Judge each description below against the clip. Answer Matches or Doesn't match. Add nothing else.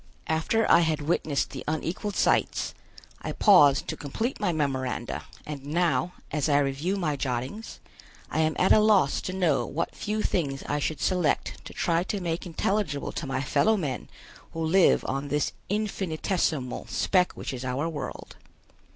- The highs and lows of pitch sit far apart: Doesn't match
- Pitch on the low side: Doesn't match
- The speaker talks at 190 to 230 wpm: Doesn't match